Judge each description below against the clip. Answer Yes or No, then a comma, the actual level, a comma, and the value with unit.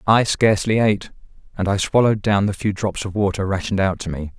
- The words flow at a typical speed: No, fast, 220 wpm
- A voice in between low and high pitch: No, low, 100 Hz